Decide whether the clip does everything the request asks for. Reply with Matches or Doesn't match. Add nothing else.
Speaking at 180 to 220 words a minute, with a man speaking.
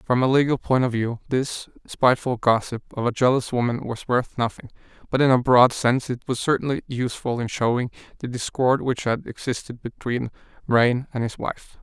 Matches